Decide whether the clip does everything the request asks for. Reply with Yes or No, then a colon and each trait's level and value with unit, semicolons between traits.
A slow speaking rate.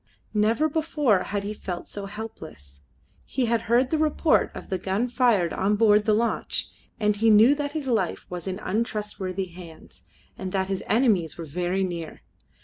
No: average, 175 wpm